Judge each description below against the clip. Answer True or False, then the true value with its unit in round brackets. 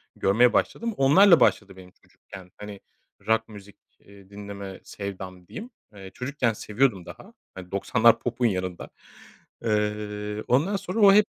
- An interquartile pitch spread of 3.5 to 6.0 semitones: True (4.2 semitones)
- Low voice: True (105 Hz)